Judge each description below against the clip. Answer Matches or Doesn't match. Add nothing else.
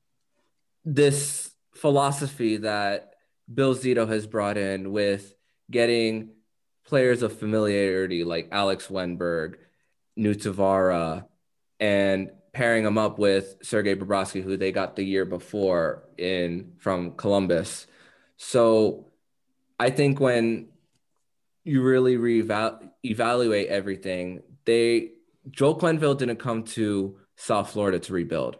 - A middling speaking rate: Doesn't match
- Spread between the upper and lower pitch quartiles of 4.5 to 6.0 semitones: Doesn't match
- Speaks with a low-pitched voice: Matches